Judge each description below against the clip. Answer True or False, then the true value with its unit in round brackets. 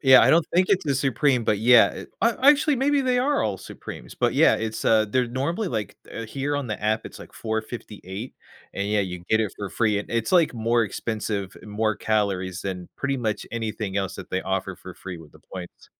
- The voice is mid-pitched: False (110 Hz)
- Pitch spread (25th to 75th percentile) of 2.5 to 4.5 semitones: False (5.0 semitones)